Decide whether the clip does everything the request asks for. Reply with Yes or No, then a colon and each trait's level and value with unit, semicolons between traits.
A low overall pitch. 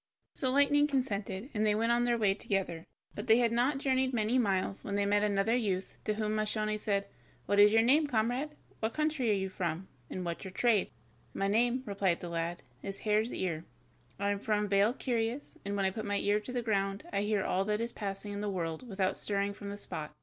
No: high, 210 Hz